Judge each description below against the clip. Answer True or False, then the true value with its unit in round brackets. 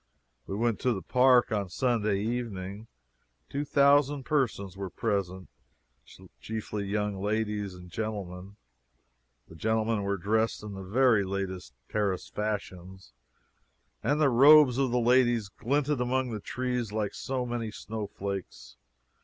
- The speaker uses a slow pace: True (130 wpm)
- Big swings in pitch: False (4.0 semitones)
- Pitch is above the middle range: False (110 Hz)